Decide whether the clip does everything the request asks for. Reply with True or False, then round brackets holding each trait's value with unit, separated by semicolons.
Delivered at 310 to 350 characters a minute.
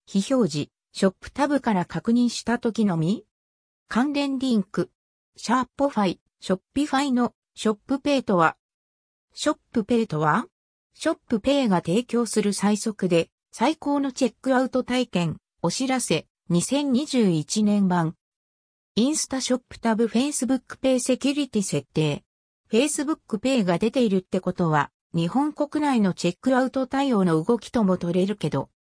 True (330 characters per minute)